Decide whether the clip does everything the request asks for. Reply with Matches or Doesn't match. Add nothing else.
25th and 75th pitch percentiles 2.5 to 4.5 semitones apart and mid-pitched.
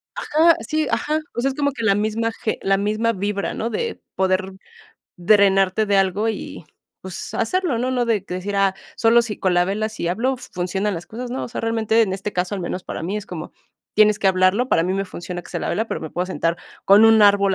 Doesn't match